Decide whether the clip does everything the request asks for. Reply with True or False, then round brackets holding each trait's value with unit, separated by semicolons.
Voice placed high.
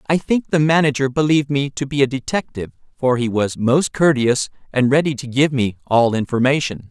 False (135 Hz)